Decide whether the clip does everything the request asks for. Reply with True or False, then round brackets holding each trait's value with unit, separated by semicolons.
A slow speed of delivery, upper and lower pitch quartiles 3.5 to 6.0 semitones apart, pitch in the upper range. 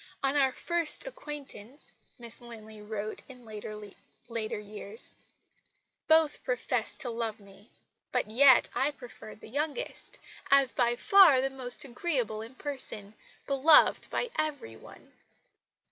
True (125 wpm; 4.7 semitones; 245 Hz)